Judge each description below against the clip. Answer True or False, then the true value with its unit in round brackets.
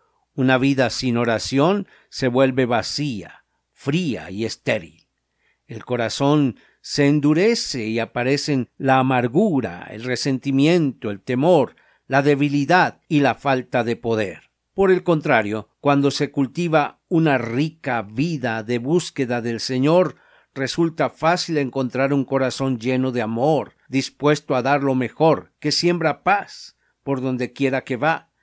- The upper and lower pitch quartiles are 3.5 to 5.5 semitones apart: False (3.1 semitones)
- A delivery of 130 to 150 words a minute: True (135 wpm)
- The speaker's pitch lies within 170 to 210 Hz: False (135 Hz)